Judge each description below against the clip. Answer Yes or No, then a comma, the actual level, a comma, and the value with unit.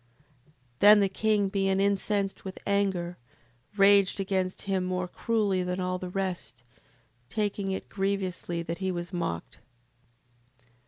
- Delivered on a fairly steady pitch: Yes, narrow, 1.6 semitones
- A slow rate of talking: Yes, slow, 130 wpm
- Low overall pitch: No, high, 190 Hz